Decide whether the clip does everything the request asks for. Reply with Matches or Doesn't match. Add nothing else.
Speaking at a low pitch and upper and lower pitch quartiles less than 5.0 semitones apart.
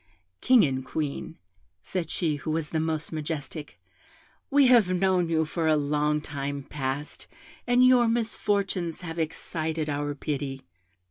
Doesn't match